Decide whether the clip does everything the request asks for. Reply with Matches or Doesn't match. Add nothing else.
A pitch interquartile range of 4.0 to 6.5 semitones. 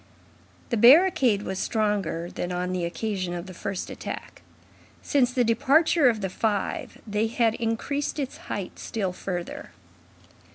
Matches